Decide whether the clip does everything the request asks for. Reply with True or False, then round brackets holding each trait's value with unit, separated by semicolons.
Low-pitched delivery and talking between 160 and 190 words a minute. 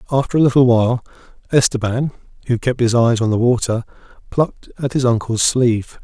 True (120 Hz; 170 wpm)